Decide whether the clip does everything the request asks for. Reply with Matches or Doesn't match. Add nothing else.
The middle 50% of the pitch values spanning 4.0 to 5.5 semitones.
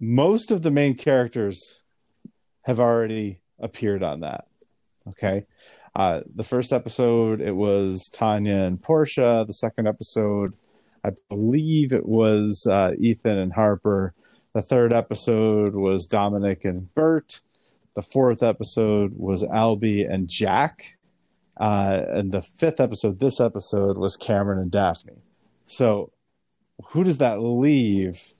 Doesn't match